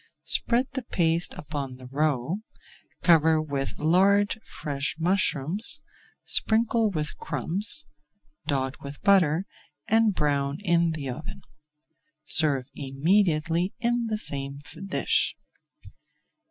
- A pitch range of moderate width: No, wide, 6.0 semitones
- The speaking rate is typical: No, slow, 100 wpm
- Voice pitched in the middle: Yes, medium, 160 Hz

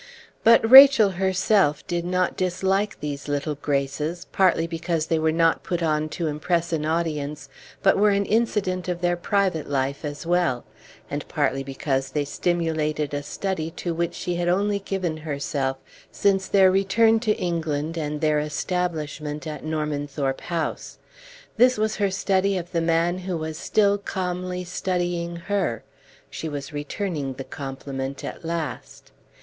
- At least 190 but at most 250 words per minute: No, average, 155 wpm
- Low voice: No, medium, 170 Hz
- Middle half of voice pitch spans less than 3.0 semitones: No, average, 3.9 semitones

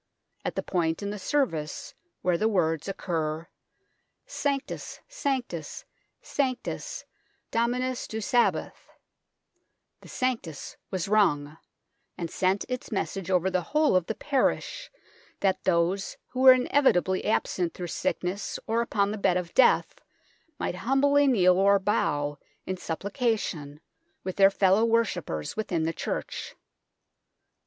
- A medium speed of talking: No, slow, 130 wpm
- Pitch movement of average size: No, wide, 6.0 semitones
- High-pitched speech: Yes, high, 195 Hz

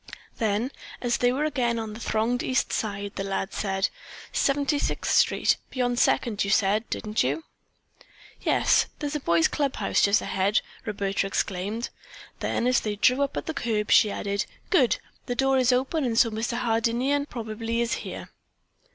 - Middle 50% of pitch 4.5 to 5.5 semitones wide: No, average, 3.7 semitones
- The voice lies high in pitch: Yes, high, 230 Hz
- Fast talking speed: No, average, 175 wpm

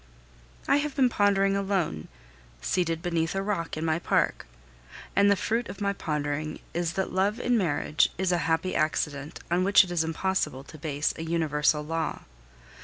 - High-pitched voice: No, medium, 170 Hz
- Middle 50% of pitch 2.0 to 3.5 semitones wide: No, average, 4.0 semitones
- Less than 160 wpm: No, average, 175 wpm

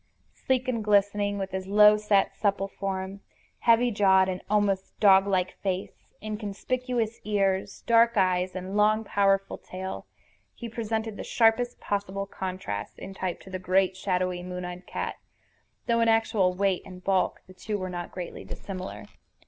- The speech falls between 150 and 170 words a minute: Yes, average, 155 wpm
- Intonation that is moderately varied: No, narrow, 2.2 semitones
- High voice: Yes, high, 195 Hz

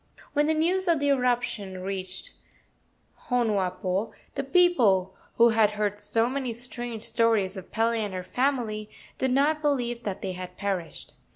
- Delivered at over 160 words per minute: No, average, 155 wpm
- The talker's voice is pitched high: Yes, high, 225 Hz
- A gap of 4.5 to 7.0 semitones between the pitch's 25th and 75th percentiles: Yes, average, 5.0 semitones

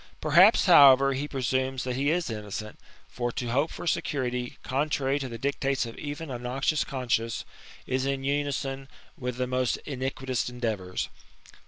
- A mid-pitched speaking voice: No, low, 130 Hz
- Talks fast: No, average, 155 wpm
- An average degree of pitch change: No, narrow, 2.3 semitones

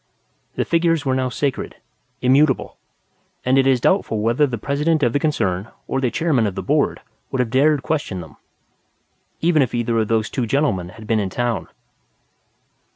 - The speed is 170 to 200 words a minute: Yes, average, 175 wpm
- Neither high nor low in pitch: No, low, 130 Hz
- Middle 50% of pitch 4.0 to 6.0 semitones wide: Yes, average, 4.3 semitones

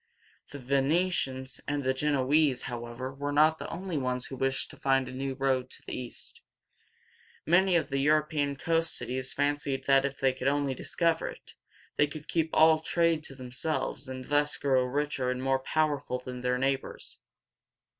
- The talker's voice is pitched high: No, medium, 140 Hz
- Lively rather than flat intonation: No, average, 2.7 semitones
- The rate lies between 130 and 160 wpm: No, average, 185 wpm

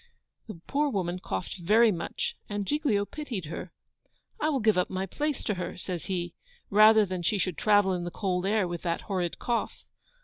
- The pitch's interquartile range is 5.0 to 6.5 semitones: No, average, 3.4 semitones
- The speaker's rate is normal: Yes, average, 195 wpm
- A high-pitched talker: Yes, high, 195 Hz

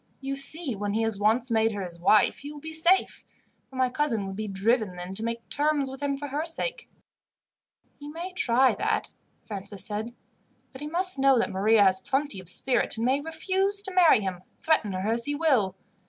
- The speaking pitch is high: Yes, very high, 255 Hz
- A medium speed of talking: No, fast, 210 wpm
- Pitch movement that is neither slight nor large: No, wide, 6.4 semitones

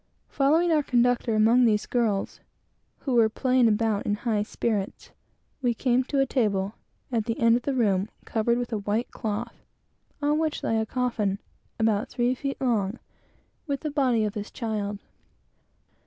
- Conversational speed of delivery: Yes, average, 170 wpm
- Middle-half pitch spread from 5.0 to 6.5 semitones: No, average, 3.0 semitones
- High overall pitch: Yes, high, 230 Hz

